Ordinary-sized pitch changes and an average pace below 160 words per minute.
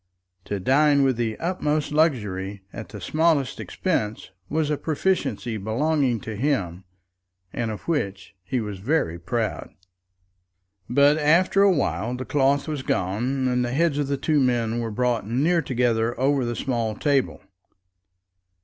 Yes: average, 5.0 semitones; average, 150 wpm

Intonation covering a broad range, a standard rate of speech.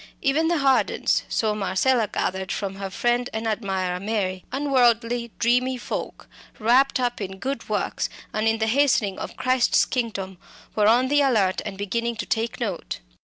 No: average, 4.2 semitones; average, 165 wpm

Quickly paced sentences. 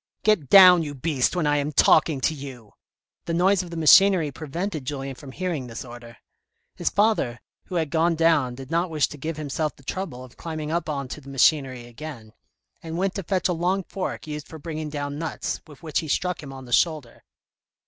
Yes: fast, 210 wpm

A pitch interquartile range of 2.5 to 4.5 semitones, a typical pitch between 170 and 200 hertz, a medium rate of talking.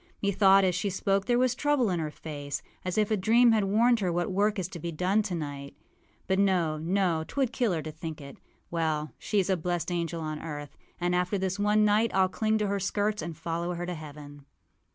No: average, 4.2 semitones; medium, 185 Hz; fast, 220 wpm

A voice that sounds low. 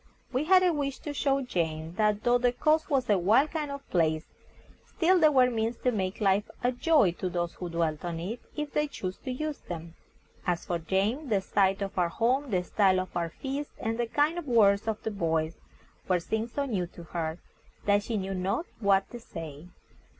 No: high, 210 Hz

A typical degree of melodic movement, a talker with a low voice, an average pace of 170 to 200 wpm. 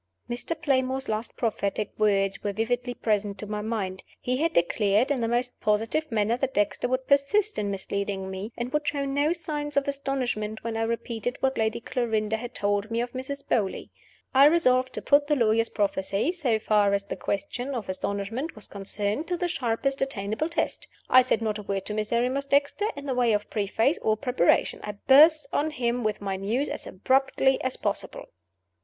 No: average, 4.6 semitones; high, 235 Hz; average, 190 wpm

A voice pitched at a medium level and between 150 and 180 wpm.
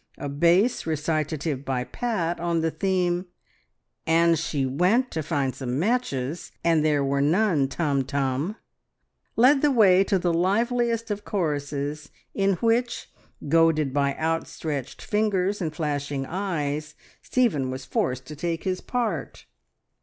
No: medium, 165 Hz; average, 140 wpm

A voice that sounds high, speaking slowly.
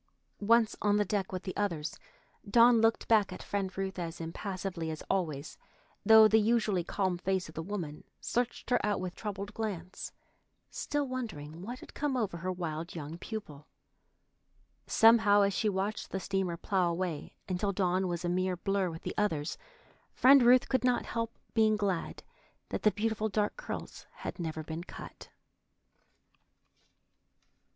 No: high, 195 Hz; average, 160 wpm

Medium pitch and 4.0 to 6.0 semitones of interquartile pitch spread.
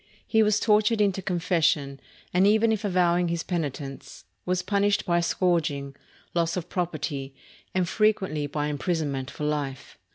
Yes: medium, 175 Hz; average, 4.7 semitones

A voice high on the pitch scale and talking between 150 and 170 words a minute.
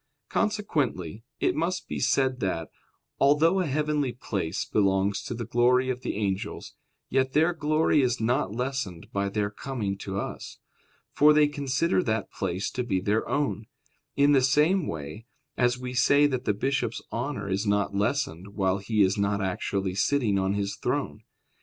No: low, 120 Hz; average, 165 wpm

